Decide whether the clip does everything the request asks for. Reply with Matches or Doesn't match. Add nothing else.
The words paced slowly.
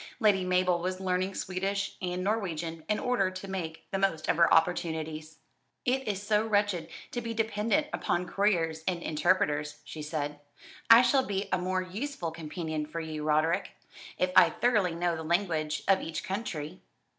Doesn't match